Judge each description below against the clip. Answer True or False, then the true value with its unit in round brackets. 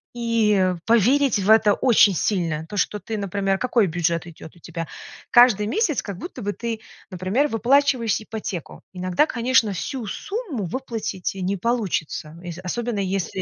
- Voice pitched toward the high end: True (210 Hz)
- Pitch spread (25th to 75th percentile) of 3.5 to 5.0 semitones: True (4.4 semitones)